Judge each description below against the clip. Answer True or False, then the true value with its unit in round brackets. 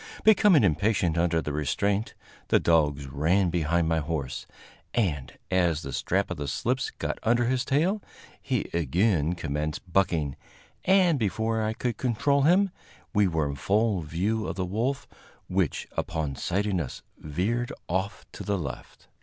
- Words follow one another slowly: False (155 wpm)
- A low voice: True (90 Hz)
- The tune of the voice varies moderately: False (6.0 semitones)